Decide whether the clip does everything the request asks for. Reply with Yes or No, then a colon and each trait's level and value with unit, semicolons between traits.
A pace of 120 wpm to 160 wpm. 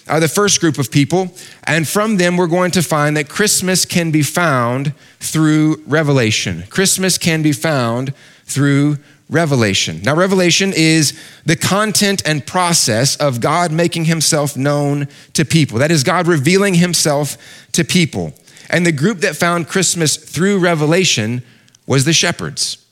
Yes: average, 150 wpm